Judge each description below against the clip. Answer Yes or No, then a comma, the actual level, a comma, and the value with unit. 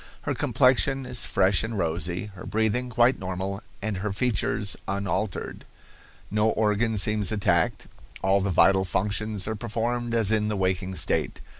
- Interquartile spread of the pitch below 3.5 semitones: Yes, average, 2.7 semitones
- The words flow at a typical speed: Yes, average, 150 wpm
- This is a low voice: Yes, low, 105 Hz